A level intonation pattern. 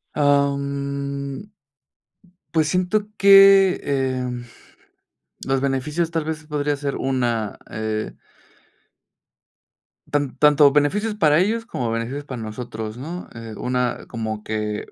No: average, 4.2 semitones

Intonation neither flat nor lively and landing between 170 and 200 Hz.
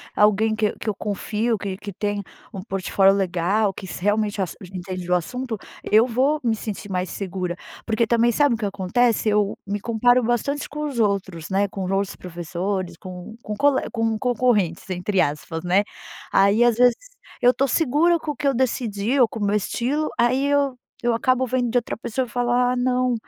No: average, 4.2 semitones; high, 220 Hz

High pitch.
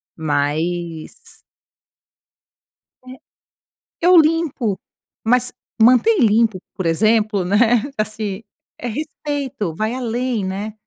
Yes: high, 220 Hz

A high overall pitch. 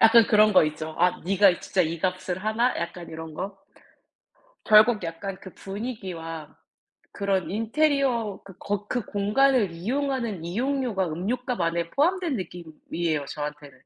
Yes: high, 195 Hz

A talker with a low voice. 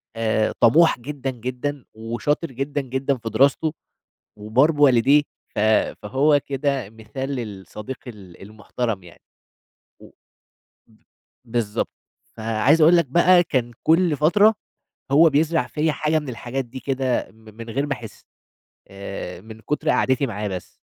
Yes: low, 130 Hz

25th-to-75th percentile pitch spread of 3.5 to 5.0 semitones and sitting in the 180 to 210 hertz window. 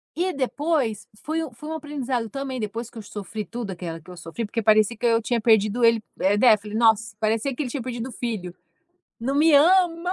No: average, 4.5 semitones; high, 230 Hz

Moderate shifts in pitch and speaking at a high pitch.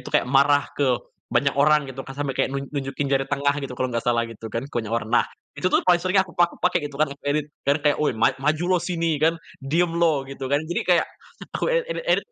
No: average, 3.7 semitones; medium, 145 Hz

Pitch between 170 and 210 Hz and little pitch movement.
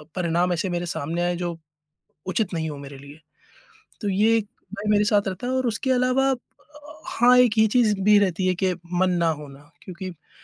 No: high, 190 Hz; average, 4.3 semitones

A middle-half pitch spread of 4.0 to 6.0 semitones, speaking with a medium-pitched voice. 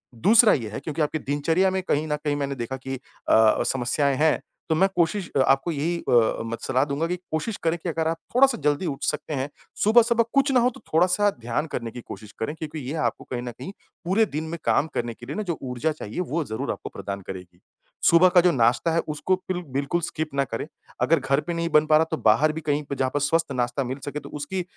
Yes: average, 4.3 semitones; medium, 150 Hz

